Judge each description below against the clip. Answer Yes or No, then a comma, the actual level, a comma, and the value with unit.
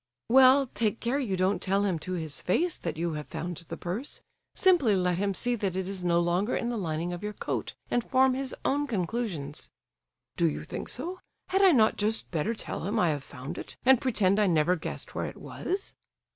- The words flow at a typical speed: No, fast, 215 wpm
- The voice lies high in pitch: Yes, high, 200 Hz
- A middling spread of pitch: No, wide, 6.0 semitones